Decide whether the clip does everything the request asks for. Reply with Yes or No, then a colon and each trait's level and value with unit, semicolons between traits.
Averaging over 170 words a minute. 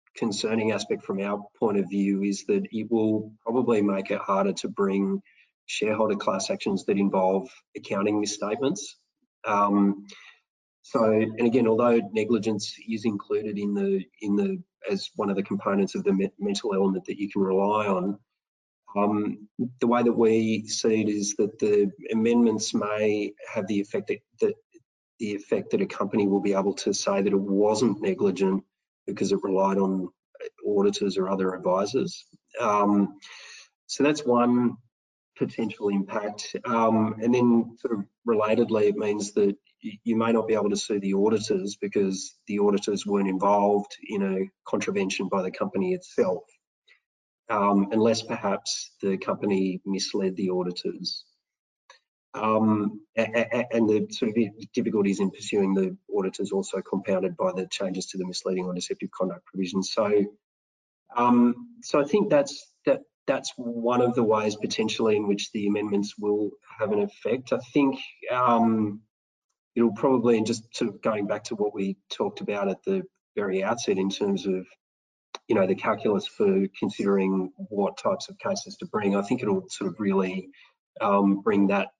No: average, 160 wpm